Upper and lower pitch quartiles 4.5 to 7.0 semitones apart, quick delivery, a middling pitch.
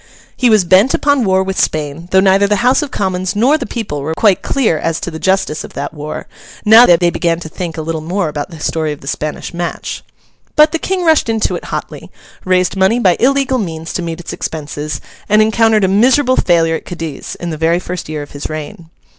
Yes: wide, 5.4 semitones; fast, 230 wpm; medium, 180 Hz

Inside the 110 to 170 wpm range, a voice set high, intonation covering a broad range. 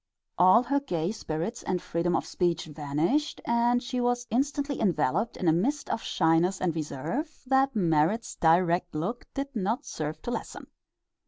Yes: average, 160 wpm; high, 195 Hz; wide, 6.7 semitones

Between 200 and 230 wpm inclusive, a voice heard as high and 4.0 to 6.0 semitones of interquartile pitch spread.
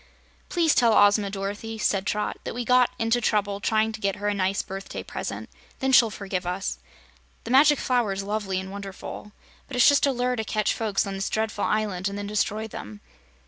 No: fast, 205 wpm; high, 210 Hz; narrow, 2.5 semitones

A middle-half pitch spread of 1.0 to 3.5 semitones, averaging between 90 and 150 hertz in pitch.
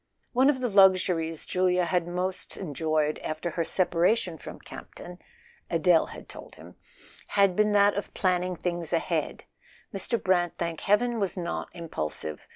No: average, 2.8 semitones; medium, 180 Hz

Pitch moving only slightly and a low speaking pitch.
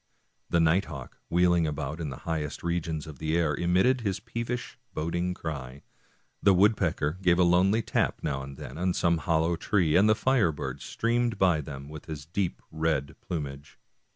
No: average, 3.6 semitones; very low, 85 Hz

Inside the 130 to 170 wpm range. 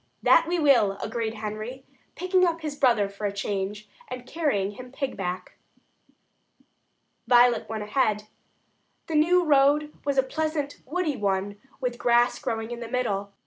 Yes: average, 150 wpm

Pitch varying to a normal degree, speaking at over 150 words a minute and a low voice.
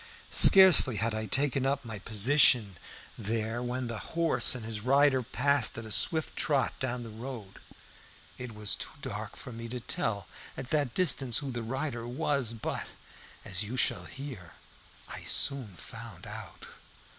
Yes: average, 3.7 semitones; average, 160 wpm; low, 120 Hz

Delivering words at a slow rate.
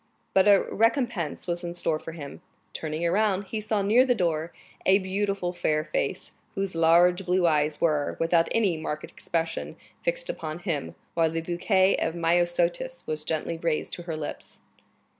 No: average, 165 wpm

